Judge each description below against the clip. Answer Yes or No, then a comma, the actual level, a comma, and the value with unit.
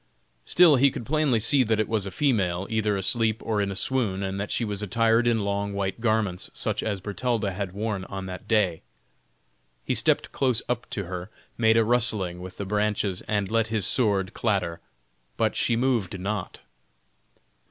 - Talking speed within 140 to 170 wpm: No, average, 185 wpm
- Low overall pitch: Yes, low, 105 Hz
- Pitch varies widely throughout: No, average, 2.9 semitones